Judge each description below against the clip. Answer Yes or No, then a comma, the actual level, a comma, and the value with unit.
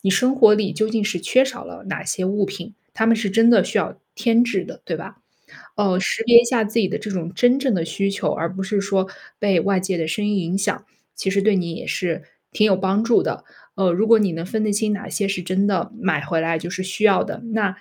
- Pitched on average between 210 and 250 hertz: No, high, 200 Hz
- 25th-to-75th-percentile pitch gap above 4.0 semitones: No, average, 2.8 semitones